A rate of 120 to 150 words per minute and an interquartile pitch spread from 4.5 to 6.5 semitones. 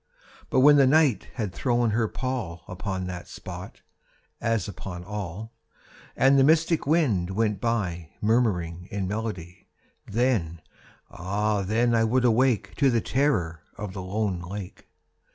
Yes: slow, 135 wpm; average, 5.0 semitones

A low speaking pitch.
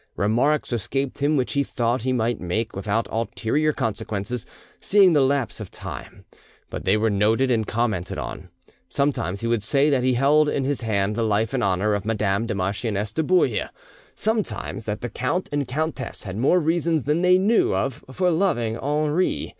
Yes: low, 120 Hz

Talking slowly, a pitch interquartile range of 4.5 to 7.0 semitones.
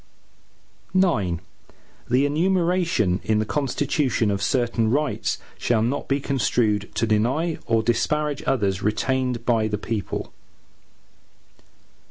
Yes: slow, 110 wpm; average, 4.9 semitones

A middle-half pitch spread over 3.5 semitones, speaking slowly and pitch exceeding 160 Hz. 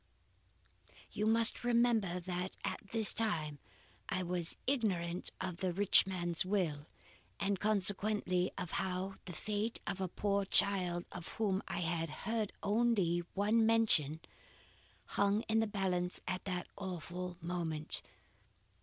No: average, 3.1 semitones; slow, 130 wpm; high, 190 Hz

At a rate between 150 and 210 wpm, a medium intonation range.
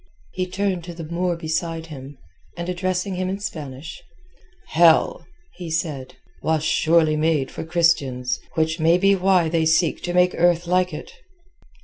No: average, 155 wpm; narrow, 2.2 semitones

